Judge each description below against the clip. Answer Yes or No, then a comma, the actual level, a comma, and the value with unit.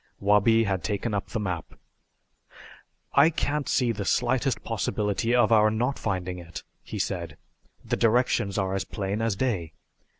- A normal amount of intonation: Yes, average, 3.6 semitones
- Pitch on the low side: Yes, low, 105 Hz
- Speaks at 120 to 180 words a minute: Yes, average, 155 wpm